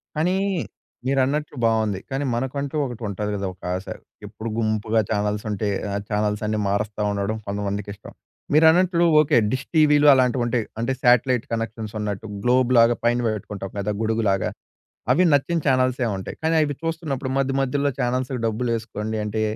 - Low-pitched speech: Yes, low, 115 Hz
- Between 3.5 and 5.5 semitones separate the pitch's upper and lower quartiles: Yes, average, 4.3 semitones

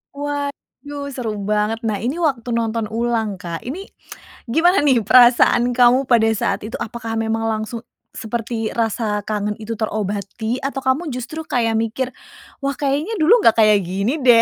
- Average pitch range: Yes, average, 3.6 semitones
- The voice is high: Yes, high, 235 Hz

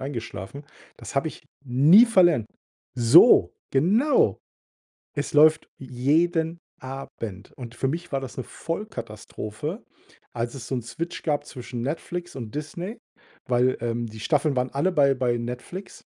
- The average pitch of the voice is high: No, low, 135 Hz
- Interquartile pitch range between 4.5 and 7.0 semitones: Yes, average, 5.3 semitones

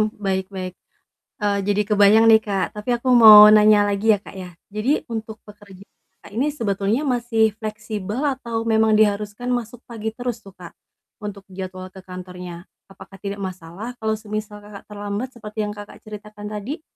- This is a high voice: Yes, high, 210 Hz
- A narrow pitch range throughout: Yes, narrow, 2.0 semitones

